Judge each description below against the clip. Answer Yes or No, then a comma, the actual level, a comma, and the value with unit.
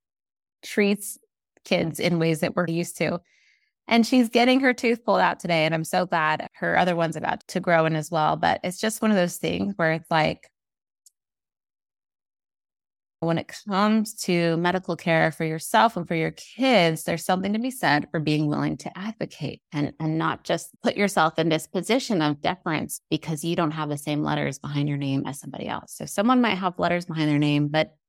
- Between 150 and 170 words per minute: No, average, 200 wpm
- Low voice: No, medium, 170 Hz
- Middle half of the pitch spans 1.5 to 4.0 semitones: No, average, 4.4 semitones